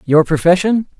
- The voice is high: No, medium, 175 Hz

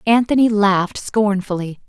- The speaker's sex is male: No, female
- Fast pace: No, slow, 95 wpm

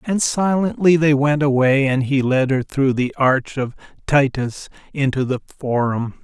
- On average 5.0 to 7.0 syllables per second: No, 4.3 syllables/s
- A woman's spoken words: No, male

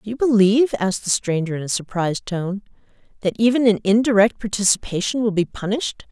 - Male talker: No, female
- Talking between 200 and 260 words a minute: No, average, 175 wpm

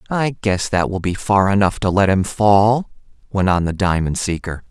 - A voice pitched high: No, low, 100 Hz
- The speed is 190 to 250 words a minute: Yes, fast, 205 wpm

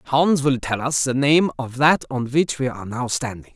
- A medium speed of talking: No, fast, 235 wpm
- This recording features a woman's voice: No, male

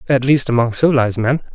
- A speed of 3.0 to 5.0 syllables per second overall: No, 7.1 syllables/s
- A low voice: Yes, low, 125 Hz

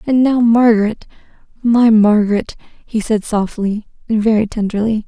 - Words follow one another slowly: Yes, slow, 120 wpm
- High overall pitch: Yes, high, 220 Hz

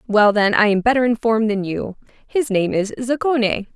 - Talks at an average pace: Yes, average, 190 wpm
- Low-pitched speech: No, high, 225 Hz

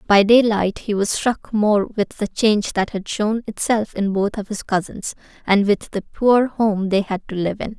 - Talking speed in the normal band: No, fast, 215 wpm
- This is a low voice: No, high, 210 Hz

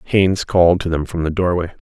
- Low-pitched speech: Yes, very low, 90 Hz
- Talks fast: Yes, fast, 225 wpm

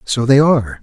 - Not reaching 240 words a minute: Yes, fast, 220 wpm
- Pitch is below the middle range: Yes, low, 125 Hz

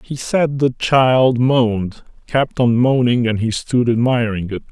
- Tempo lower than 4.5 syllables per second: Yes, 4.0 syllables/s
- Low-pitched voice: Yes, low, 120 Hz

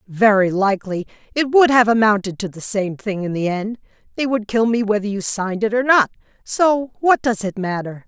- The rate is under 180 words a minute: No, average, 200 wpm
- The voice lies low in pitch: No, high, 215 Hz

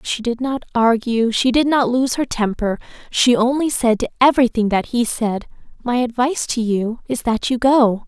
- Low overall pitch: No, high, 240 Hz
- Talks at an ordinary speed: Yes, average, 195 wpm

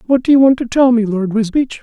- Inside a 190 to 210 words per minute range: No, fast, 295 wpm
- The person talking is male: Yes, male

